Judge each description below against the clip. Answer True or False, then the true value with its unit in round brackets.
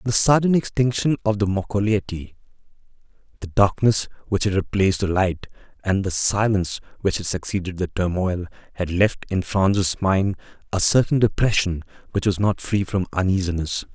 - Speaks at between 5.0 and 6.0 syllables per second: True (5.1 syllables/s)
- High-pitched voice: False (100 Hz)